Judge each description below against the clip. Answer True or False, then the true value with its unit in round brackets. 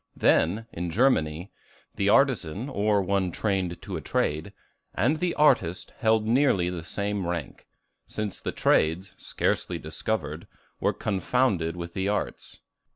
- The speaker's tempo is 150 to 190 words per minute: False (135 wpm)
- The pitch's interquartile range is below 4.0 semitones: False (4.4 semitones)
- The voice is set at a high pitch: False (95 Hz)